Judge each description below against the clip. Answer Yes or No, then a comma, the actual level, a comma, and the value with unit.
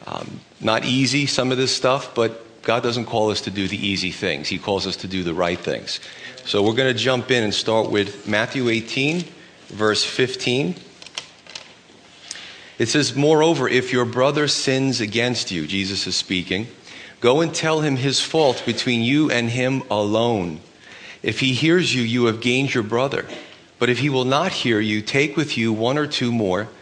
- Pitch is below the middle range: Yes, low, 120 Hz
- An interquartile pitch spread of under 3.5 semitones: No, average, 4.0 semitones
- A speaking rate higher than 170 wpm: Yes, average, 190 wpm